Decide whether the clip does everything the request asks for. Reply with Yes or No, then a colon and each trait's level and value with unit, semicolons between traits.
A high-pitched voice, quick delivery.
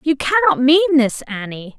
No: very high, 270 Hz; average, 170 wpm